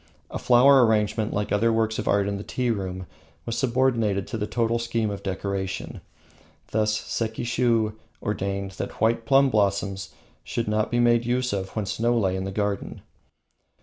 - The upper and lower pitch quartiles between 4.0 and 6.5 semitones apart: No, average, 2.8 semitones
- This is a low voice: Yes, low, 110 Hz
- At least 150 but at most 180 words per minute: Yes, average, 175 wpm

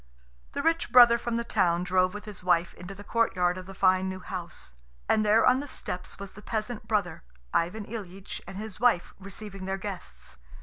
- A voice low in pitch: No, high, 195 Hz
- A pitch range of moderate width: Yes, average, 3.1 semitones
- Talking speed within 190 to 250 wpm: Yes, average, 200 wpm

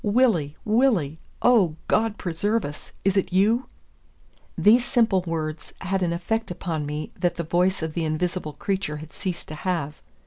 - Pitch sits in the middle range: Yes, medium, 180 Hz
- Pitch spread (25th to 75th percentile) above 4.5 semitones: Yes, average, 5.0 semitones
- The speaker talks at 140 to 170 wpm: Yes, average, 165 wpm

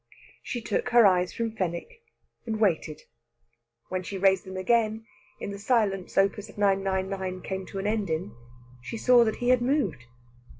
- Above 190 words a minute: No, average, 165 wpm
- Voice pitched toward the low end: No, high, 195 Hz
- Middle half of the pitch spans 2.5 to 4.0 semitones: Yes, average, 3.1 semitones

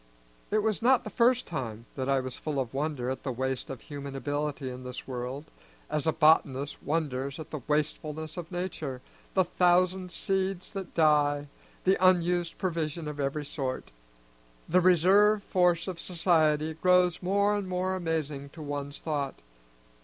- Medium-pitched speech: Yes, medium, 155 Hz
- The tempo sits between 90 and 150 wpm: No, average, 160 wpm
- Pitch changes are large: No, average, 4.5 semitones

